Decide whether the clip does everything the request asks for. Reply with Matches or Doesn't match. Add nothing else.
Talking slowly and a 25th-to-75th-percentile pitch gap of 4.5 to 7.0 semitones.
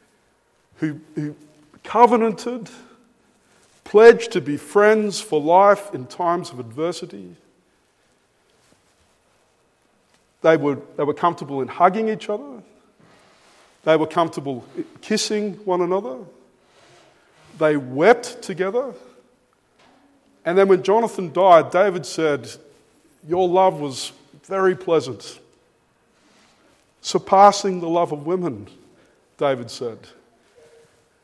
Matches